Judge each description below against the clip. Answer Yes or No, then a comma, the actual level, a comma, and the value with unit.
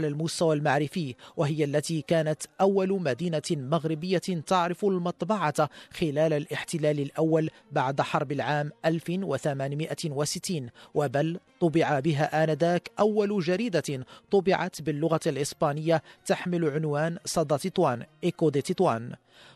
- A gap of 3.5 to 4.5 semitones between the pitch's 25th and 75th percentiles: No, average, 2.8 semitones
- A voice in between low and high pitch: Yes, medium, 160 Hz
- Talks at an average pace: Yes, average, 100 wpm